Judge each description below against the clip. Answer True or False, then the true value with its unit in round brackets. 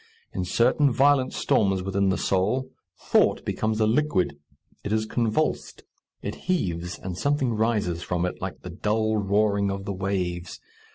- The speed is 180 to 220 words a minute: False (155 wpm)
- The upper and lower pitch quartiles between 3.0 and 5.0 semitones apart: True (3.6 semitones)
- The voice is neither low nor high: False (100 Hz)